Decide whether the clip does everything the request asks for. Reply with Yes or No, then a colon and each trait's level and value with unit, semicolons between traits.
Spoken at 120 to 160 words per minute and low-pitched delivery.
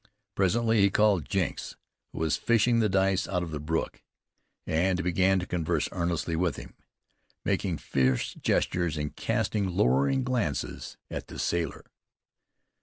Yes: average, 140 wpm; very low, 90 Hz